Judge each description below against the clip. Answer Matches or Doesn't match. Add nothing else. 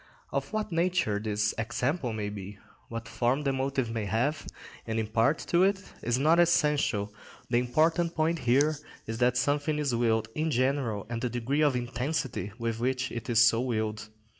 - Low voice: Matches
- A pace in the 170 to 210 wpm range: Matches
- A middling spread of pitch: Matches